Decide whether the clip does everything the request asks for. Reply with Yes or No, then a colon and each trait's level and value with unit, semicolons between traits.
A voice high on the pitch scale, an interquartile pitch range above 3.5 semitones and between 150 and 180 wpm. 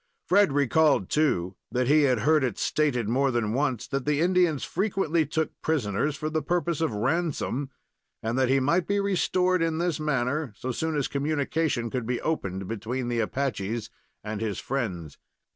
No: medium, 140 Hz; average, 5.0 semitones; average, 175 wpm